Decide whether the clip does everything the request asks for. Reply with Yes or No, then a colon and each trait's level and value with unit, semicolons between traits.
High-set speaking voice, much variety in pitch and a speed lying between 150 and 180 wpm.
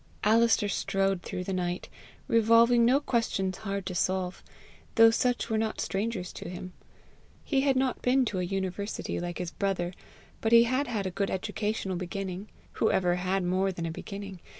No: high, 195 Hz; average, 3.8 semitones; average, 175 wpm